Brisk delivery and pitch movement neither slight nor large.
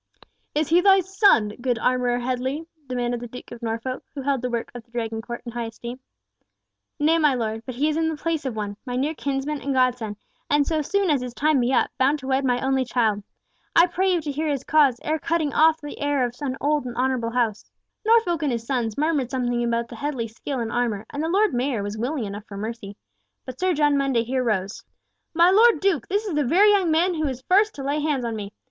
Yes: fast, 240 wpm; average, 4.4 semitones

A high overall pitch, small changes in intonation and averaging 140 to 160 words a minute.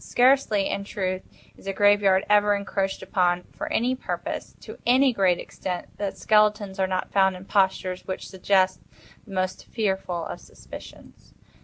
Yes: high, 195 Hz; narrow, 1.8 semitones; average, 155 wpm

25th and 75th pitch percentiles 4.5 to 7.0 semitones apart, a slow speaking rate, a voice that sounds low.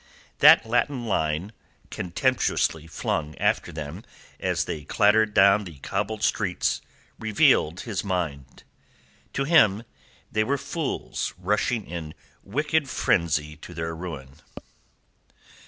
Yes: wide, 5.6 semitones; slow, 110 wpm; very low, 95 Hz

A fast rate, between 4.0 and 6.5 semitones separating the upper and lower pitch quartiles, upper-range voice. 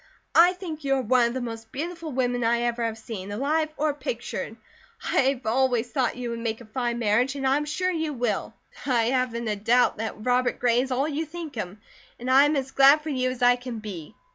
No: fast, 235 wpm; average, 3.3 semitones; very high, 250 Hz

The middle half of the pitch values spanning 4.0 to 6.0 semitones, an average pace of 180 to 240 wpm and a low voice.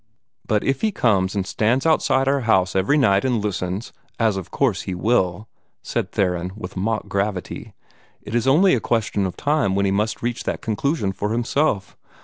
Yes: average, 4.7 semitones; average, 185 wpm; low, 105 Hz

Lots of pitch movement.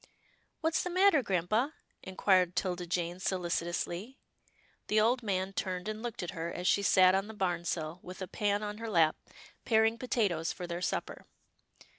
No: average, 3.9 semitones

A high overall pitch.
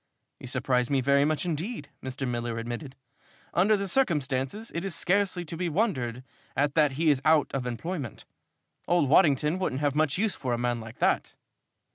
No: medium, 145 Hz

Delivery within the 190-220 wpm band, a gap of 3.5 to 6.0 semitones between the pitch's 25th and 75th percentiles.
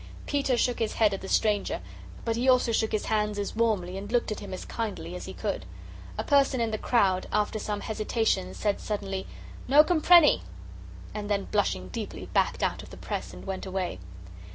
No: average, 200 wpm; average, 3.0 semitones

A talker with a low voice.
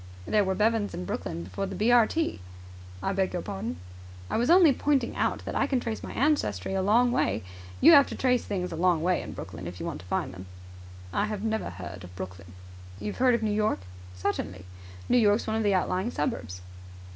No: high, 200 Hz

